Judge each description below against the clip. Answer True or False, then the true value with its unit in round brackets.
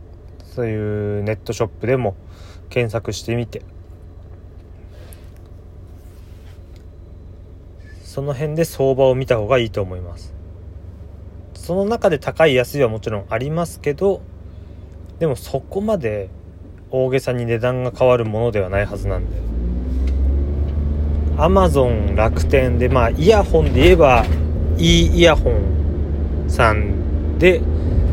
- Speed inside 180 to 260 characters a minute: True (230 characters per minute)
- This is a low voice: True (90 Hz)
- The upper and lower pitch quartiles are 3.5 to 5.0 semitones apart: False (5.5 semitones)